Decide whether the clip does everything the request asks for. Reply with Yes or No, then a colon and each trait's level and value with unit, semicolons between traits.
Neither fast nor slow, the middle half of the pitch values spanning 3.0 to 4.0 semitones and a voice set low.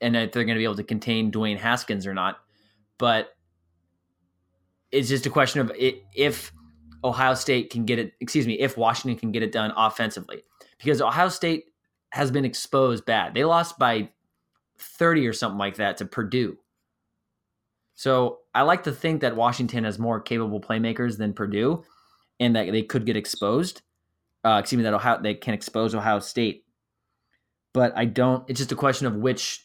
Yes: average, 180 wpm; average, 3.6 semitones; low, 115 Hz